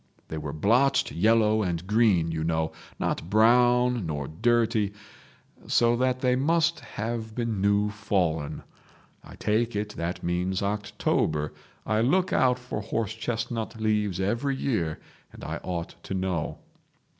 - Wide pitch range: No, average, 4.6 semitones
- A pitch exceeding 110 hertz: No, low, 105 Hz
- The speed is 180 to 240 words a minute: No, average, 140 wpm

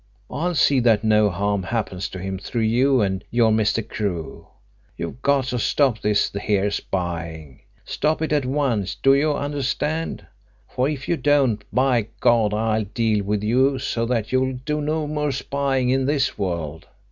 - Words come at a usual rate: Yes, average, 170 wpm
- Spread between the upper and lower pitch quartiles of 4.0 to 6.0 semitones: Yes, average, 5.2 semitones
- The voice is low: Yes, low, 115 Hz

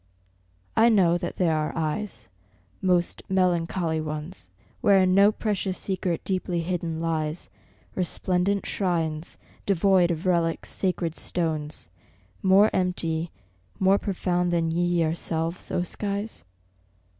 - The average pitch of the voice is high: No, medium, 175 Hz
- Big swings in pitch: No, narrow, 2.4 semitones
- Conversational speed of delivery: No, slow, 110 wpm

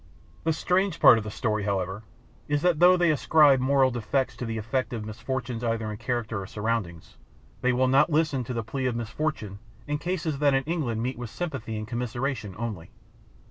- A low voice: Yes, low, 125 Hz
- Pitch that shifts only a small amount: No, average, 4.8 semitones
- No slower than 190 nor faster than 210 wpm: Yes, average, 195 wpm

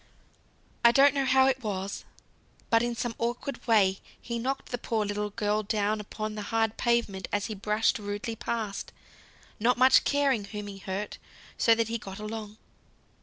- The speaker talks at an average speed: Yes, average, 170 wpm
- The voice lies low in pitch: No, high, 220 Hz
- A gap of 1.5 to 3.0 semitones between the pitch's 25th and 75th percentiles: Yes, narrow, 2.5 semitones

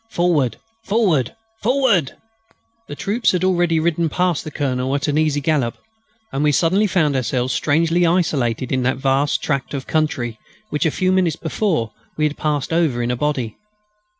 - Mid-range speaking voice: Yes, medium, 150 Hz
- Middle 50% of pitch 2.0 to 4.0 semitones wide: No, average, 4.5 semitones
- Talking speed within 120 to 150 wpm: No, average, 170 wpm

